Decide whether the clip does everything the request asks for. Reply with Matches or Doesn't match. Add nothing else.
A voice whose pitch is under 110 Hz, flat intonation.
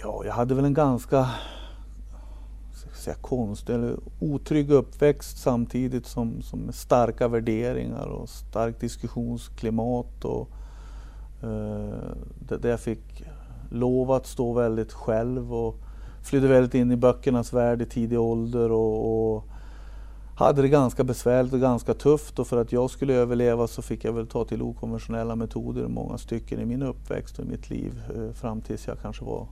Doesn't match